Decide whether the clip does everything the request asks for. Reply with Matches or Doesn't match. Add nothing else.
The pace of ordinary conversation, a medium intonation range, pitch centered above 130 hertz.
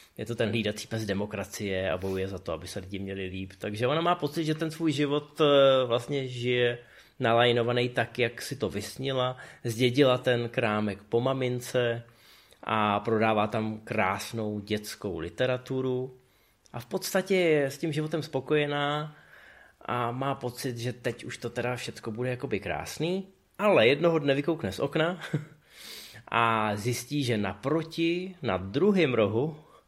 Doesn't match